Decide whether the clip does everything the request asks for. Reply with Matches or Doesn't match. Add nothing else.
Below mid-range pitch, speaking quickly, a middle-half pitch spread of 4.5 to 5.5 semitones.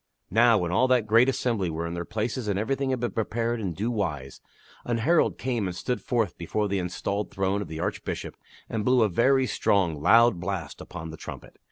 Matches